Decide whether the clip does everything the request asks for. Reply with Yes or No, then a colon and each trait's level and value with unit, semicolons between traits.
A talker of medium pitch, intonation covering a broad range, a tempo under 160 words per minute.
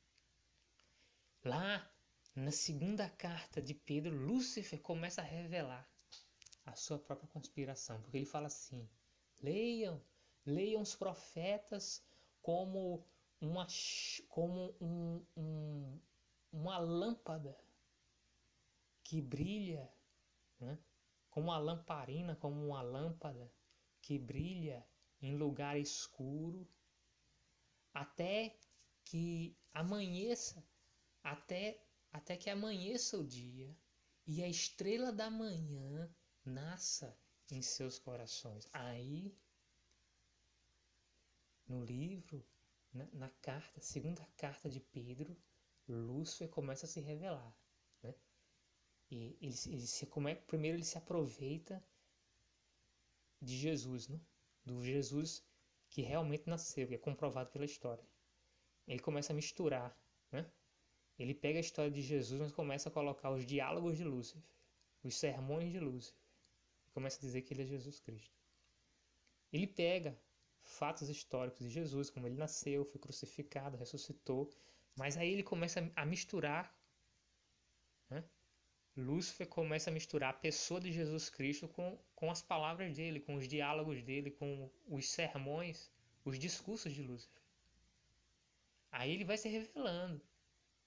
No: medium, 150 Hz; average, 4.2 semitones; slow, 120 wpm